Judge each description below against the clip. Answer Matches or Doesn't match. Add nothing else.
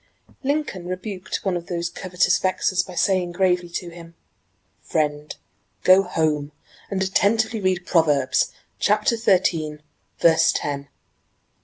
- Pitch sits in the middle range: Matches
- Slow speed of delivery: Matches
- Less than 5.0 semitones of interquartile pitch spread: Matches